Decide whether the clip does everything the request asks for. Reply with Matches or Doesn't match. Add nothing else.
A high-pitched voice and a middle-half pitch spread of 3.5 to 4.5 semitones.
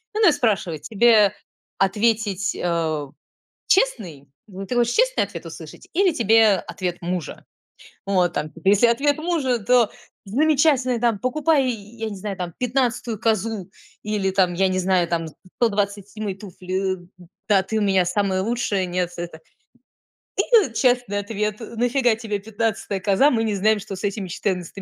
Matches